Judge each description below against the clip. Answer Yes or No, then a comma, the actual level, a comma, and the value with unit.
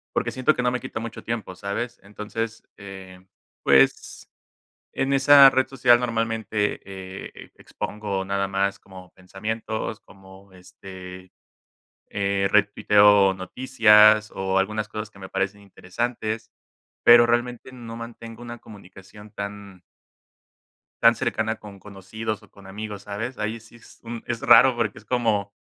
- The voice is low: Yes, low, 105 Hz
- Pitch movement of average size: Yes, average, 3.0 semitones